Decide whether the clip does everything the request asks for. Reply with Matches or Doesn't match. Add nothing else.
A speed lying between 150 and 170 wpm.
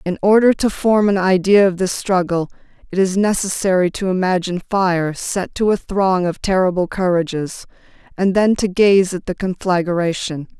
Matches